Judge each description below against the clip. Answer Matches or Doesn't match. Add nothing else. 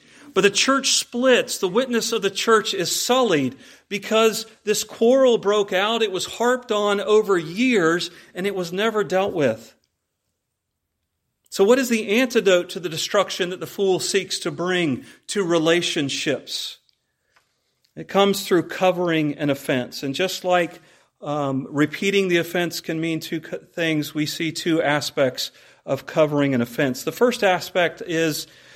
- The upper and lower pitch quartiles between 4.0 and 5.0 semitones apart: Matches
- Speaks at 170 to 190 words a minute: Doesn't match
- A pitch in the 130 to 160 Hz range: Doesn't match